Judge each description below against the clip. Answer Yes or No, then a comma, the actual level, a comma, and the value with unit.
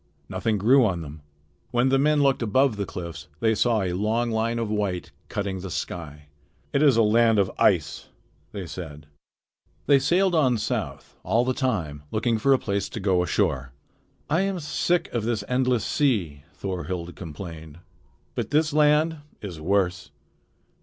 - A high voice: No, low, 110 Hz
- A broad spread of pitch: Yes, wide, 6.5 semitones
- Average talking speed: Yes, average, 165 wpm